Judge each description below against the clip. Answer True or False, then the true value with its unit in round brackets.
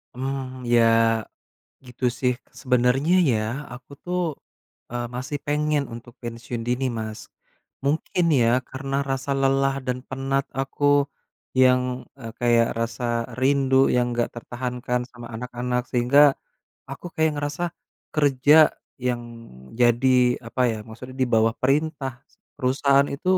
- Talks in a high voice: False (130 Hz)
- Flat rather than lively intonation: True (2.2 semitones)